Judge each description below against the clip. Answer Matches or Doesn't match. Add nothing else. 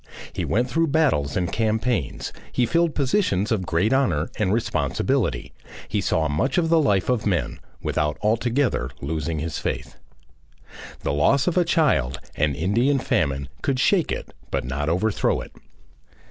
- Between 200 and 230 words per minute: Doesn't match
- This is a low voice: Matches